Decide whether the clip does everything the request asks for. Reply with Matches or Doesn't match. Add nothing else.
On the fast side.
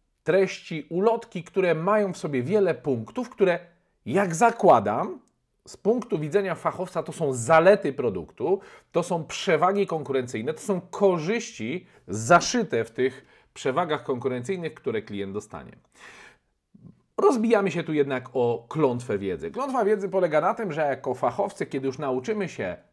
Doesn't match